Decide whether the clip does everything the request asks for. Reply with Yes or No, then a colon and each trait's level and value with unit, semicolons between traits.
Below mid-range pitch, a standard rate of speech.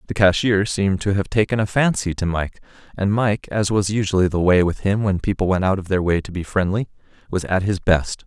No: very low, 95 Hz; fast, 240 wpm